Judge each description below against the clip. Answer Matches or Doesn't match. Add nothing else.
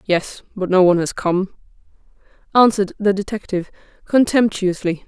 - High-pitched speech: Matches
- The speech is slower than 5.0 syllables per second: Doesn't match